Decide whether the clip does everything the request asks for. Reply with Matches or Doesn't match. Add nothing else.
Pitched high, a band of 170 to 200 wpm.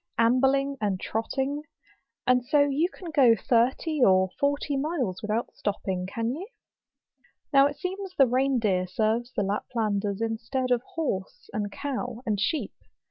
Doesn't match